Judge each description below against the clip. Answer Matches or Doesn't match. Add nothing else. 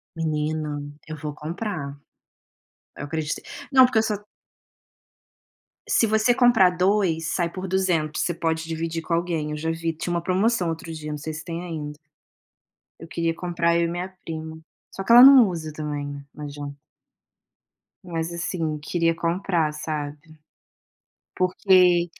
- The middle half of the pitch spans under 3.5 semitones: Matches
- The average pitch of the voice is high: Doesn't match